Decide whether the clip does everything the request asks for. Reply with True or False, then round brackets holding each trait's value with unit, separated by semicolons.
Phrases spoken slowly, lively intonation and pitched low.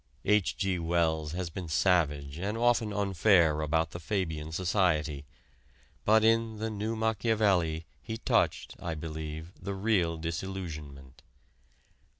False (125 wpm; 4.8 semitones; 90 Hz)